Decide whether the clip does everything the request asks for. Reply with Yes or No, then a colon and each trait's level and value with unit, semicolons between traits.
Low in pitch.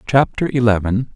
Yes: low, 120 Hz